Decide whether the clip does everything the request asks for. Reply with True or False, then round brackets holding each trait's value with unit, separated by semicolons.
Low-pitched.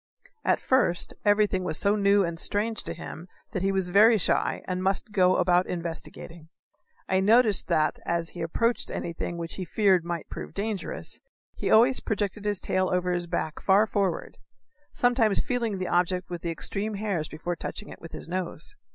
False (190 Hz)